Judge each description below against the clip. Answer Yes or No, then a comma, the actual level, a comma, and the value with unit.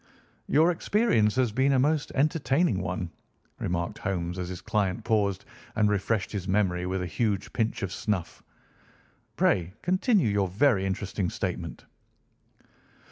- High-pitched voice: No, low, 105 Hz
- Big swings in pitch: Yes, wide, 6.0 semitones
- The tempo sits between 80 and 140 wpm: Yes, slow, 135 wpm